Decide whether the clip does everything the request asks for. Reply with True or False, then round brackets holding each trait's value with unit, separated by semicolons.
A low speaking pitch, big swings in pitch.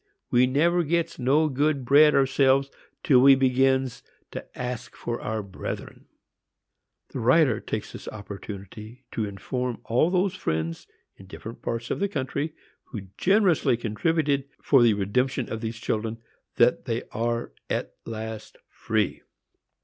False (125 Hz; 4.2 semitones)